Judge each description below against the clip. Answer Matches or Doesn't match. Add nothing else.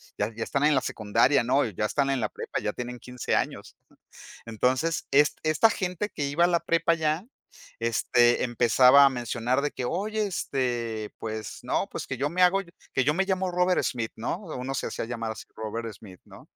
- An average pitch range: Doesn't match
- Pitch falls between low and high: Doesn't match